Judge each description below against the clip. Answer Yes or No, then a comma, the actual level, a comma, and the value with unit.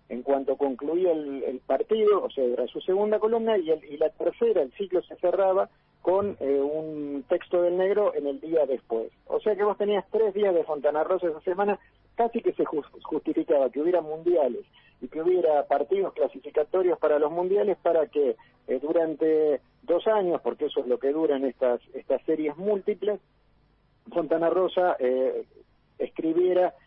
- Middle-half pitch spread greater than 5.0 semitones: Yes, wide, 5.4 semitones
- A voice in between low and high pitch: Yes, medium, 175 Hz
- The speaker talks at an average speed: Yes, average, 175 wpm